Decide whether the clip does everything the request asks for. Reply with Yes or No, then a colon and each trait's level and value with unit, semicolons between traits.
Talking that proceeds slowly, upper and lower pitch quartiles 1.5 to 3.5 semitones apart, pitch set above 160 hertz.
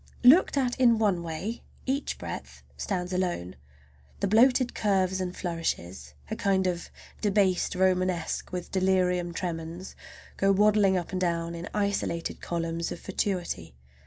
Yes: slow, 130 wpm; average, 2.9 semitones; medium, 185 Hz